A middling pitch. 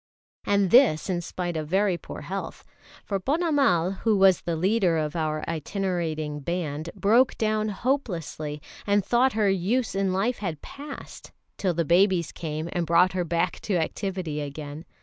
Yes: medium, 180 Hz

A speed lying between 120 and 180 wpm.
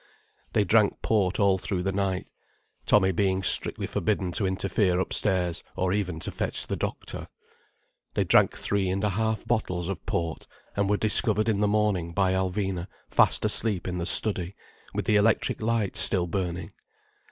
Yes: average, 165 wpm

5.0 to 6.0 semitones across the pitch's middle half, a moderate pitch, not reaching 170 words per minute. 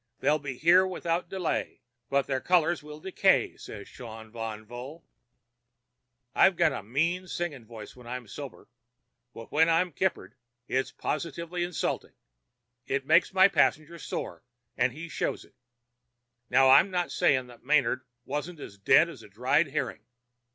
Yes: wide, 5.4 semitones; medium, 150 Hz; average, 155 wpm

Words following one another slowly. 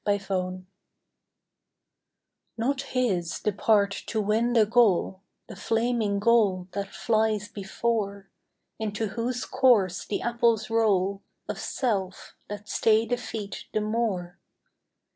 Yes: slow, 115 wpm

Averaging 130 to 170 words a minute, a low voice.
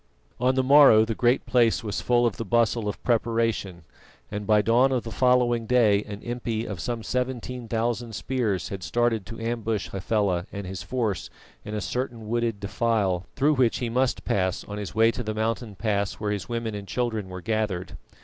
No: average, 195 wpm; low, 115 Hz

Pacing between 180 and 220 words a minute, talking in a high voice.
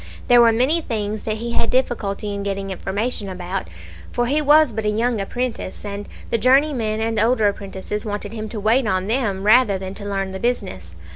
Yes: average, 200 wpm; high, 215 Hz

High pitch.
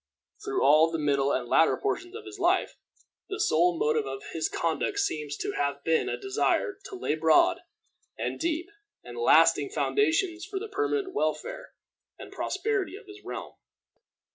Yes: very high, 355 Hz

